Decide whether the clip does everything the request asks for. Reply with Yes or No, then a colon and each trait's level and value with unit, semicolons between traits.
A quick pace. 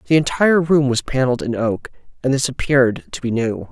Yes: fast, 210 wpm